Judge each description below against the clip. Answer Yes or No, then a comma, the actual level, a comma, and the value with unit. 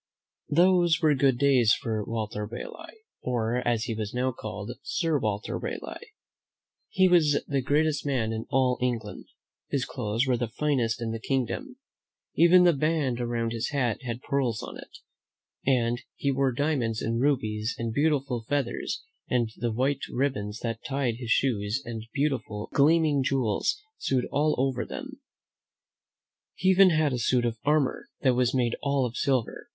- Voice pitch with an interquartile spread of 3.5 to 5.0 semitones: Yes, average, 3.8 semitones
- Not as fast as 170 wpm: Yes, average, 160 wpm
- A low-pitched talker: Yes, low, 130 Hz